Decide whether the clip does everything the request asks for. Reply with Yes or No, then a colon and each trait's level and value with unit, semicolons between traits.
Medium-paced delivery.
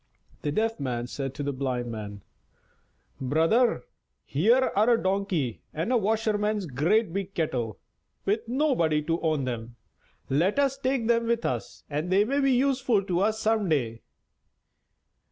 Yes: average, 150 wpm